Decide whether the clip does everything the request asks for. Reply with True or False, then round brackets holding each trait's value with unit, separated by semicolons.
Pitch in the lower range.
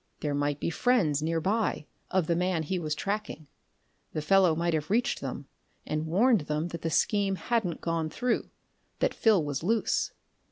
False (170 Hz)